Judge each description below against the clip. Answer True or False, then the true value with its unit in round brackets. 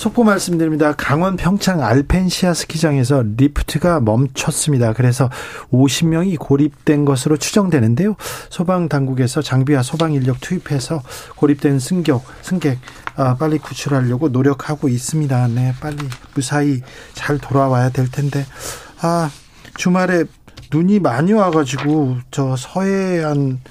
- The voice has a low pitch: False (145 Hz)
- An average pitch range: True (3.7 semitones)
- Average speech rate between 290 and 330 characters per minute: True (295 characters per minute)